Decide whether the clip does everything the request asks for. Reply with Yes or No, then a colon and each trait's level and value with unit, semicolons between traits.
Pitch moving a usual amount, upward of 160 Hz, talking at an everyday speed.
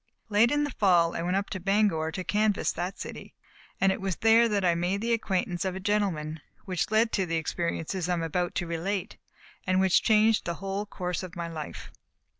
No: average, 3.2 semitones; high, 190 Hz; fast, 220 wpm